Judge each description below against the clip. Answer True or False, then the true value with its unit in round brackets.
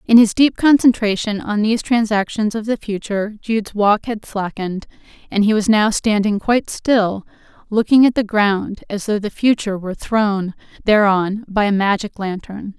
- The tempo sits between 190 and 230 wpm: False (170 wpm)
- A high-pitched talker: True (210 Hz)